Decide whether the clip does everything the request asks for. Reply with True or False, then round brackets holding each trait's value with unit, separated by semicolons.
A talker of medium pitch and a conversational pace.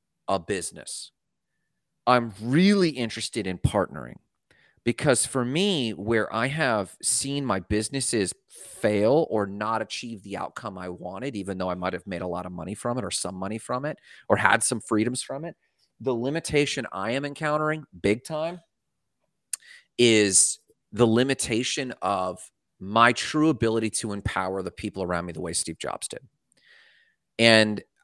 False (115 Hz; 155 wpm)